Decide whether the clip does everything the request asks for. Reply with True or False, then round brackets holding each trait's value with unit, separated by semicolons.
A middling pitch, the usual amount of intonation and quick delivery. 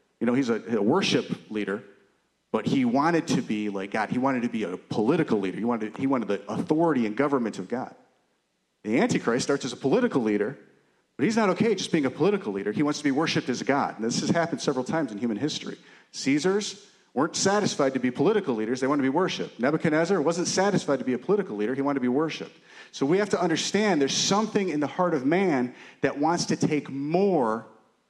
False (150 Hz; 7.9 semitones; 230 wpm)